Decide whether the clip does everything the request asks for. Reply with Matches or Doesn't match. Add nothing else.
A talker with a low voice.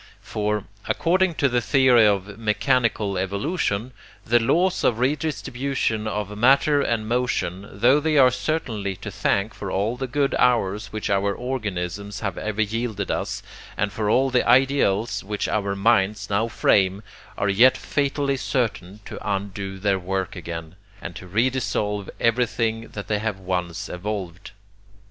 Matches